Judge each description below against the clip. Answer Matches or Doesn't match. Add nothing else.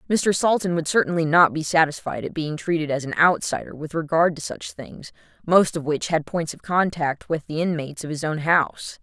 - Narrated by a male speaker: Doesn't match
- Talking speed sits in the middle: Doesn't match